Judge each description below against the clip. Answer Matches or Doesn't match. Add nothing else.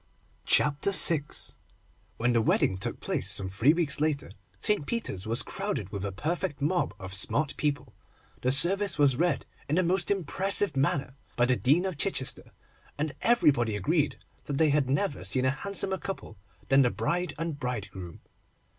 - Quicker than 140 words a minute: Matches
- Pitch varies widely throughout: Matches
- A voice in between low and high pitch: Matches